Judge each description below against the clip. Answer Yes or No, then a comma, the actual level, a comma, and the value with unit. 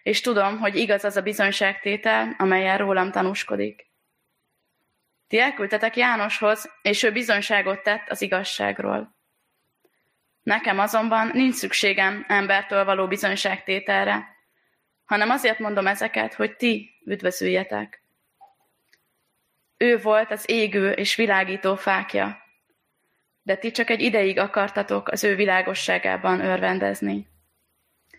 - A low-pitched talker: No, high, 200 Hz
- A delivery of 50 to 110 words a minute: Yes, slow, 105 wpm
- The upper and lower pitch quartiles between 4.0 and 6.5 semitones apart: No, narrow, 2.4 semitones